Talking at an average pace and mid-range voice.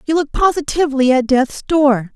No: average, 165 wpm; very high, 280 Hz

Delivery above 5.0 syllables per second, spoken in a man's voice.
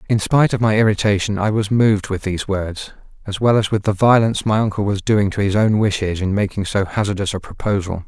Yes: 6.1 syllables/s; male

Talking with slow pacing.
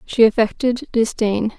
Yes: slow, 115 wpm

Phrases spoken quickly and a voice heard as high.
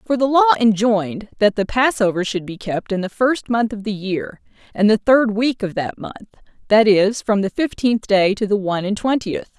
Yes: fast, 220 wpm; high, 215 Hz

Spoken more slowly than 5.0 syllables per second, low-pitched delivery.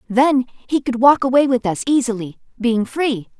No: 4.6 syllables/s; high, 245 Hz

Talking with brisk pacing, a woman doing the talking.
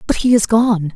Yes: fast, 250 wpm; female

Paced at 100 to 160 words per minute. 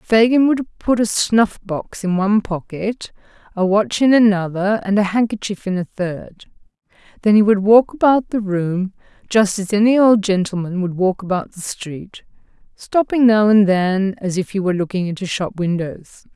No: average, 175 wpm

